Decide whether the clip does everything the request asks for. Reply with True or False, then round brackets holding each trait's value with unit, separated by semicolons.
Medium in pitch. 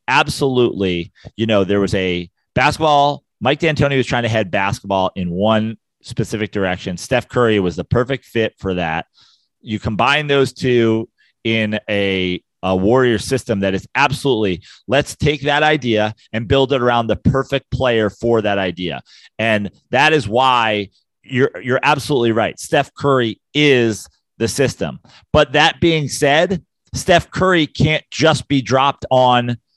False (120 Hz)